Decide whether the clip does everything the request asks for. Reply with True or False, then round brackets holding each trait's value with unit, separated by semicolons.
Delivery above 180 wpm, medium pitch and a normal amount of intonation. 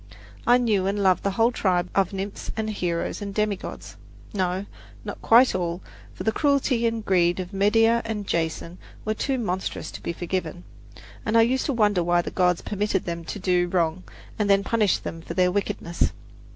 False (190 wpm; 195 Hz; 3.6 semitones)